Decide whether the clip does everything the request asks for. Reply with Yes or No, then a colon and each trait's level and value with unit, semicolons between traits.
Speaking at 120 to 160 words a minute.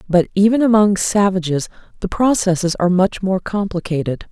Yes: average, 140 wpm